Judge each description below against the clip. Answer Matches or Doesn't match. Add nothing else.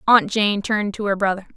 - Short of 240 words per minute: Matches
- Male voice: Doesn't match